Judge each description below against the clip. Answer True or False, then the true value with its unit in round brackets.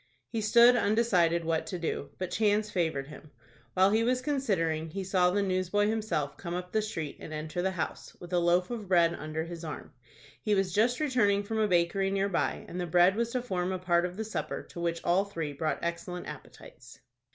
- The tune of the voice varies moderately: True (3.6 semitones)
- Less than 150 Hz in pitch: False (185 Hz)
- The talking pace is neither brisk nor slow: False (215 wpm)